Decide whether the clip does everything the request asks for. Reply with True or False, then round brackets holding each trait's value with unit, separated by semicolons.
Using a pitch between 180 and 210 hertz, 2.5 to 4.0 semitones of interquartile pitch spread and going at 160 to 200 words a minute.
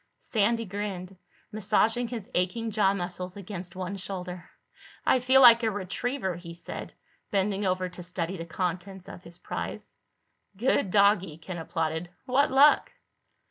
False (190 Hz; 3.4 semitones; 140 wpm)